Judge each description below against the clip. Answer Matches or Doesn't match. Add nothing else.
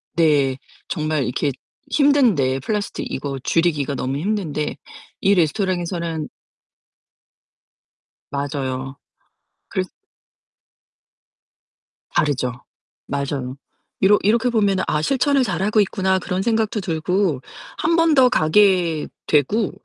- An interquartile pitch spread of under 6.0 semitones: Doesn't match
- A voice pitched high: Doesn't match